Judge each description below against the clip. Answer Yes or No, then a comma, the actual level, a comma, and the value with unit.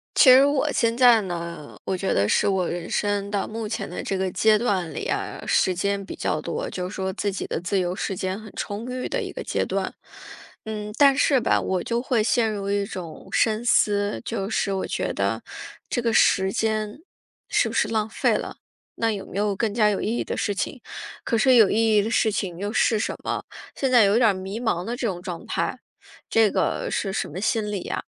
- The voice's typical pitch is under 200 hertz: No, high, 210 Hz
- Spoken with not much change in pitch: No, average, 3.0 semitones